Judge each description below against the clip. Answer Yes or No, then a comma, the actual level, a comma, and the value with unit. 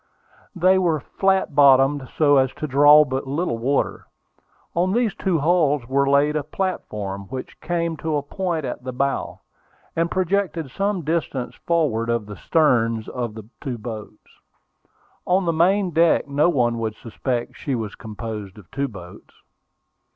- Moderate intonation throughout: No, wide, 6.1 semitones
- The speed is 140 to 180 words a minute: Yes, average, 160 wpm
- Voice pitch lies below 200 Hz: Yes, medium, 140 Hz